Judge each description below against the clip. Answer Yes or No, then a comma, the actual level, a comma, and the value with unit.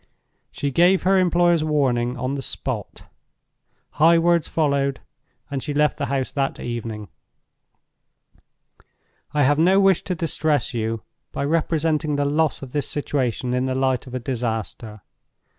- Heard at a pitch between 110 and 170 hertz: Yes, medium, 140 Hz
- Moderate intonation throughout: Yes, average, 4.0 semitones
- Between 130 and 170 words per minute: Yes, average, 145 wpm